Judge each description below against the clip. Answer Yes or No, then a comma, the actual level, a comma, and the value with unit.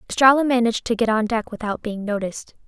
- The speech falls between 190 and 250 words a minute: Yes, average, 200 wpm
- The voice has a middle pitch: No, high, 225 Hz